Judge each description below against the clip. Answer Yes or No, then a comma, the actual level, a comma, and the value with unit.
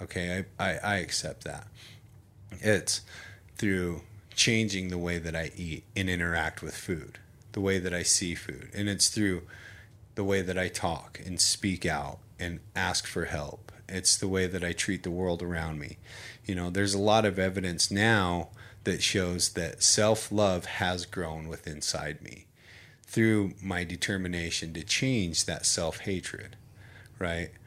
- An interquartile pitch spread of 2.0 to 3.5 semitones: Yes, average, 3.2 semitones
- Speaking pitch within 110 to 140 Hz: No, very low, 95 Hz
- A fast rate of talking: No, average, 165 wpm